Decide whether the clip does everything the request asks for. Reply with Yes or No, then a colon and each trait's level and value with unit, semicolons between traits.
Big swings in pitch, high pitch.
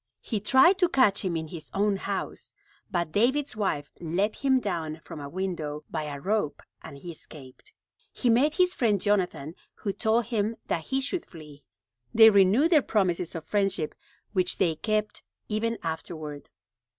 Yes: wide, 5.9 semitones; high, 195 Hz